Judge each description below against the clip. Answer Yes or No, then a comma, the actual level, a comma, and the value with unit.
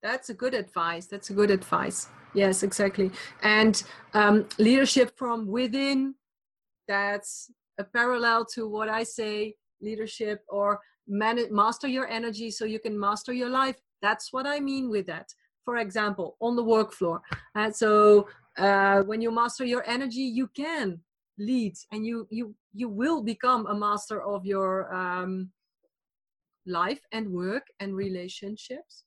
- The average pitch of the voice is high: Yes, high, 215 Hz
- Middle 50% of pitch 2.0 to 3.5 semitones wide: Yes, average, 3.1 semitones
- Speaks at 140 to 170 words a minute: Yes, average, 150 wpm